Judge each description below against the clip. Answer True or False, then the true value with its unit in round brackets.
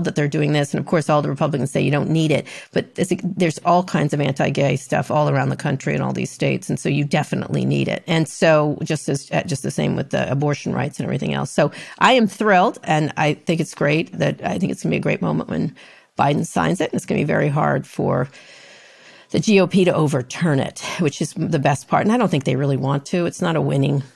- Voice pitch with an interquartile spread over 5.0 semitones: False (3.6 semitones)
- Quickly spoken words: True (260 wpm)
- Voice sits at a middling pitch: True (155 Hz)